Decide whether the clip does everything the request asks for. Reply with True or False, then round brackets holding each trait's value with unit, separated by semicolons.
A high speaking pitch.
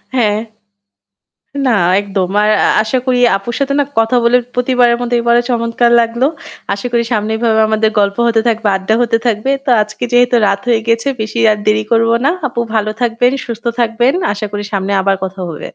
True (230 Hz)